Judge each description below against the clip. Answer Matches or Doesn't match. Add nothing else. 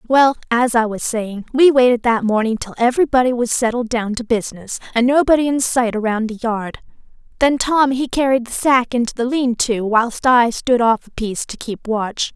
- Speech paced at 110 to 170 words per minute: Doesn't match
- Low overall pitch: Doesn't match